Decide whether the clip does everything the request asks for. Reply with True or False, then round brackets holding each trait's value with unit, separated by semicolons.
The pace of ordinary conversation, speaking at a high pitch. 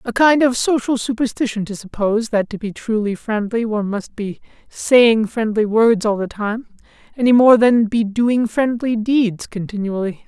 True (170 wpm; 225 Hz)